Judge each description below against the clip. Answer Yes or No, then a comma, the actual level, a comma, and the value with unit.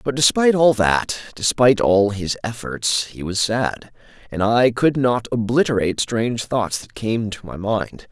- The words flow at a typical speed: Yes, average, 170 wpm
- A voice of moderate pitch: No, low, 115 Hz